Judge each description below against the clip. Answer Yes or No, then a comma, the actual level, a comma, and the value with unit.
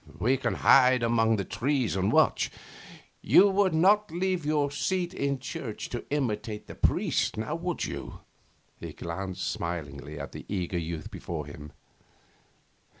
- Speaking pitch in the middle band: No, low, 115 Hz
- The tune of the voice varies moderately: No, wide, 9.0 semitones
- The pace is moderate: Yes, average, 145 wpm